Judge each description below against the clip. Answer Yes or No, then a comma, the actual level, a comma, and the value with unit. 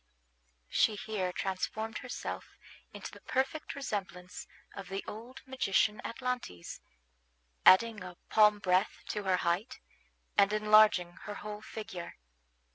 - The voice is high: Yes, high, 210 Hz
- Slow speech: Yes, slow, 120 wpm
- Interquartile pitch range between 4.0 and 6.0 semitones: No, average, 3.1 semitones